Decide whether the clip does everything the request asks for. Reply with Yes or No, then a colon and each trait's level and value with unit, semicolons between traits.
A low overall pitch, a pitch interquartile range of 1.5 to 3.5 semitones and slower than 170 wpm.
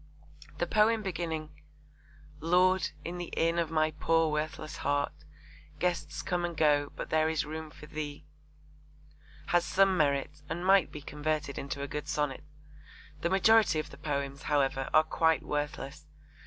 No: medium, 155 Hz; average, 2.7 semitones; average, 155 wpm